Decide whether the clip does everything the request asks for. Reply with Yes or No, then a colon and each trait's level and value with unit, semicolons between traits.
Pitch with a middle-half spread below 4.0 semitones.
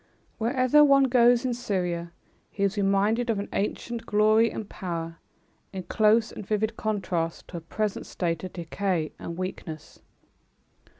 No: average, 4.4 semitones